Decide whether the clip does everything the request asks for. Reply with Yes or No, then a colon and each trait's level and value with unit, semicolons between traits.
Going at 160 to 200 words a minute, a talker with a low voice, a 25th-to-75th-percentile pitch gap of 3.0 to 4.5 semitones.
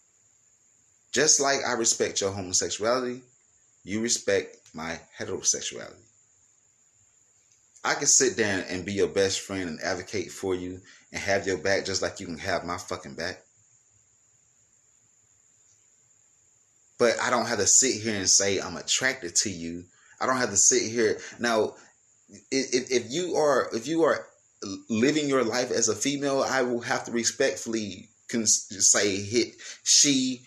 No: average, 150 wpm; low, 115 Hz; average, 3.5 semitones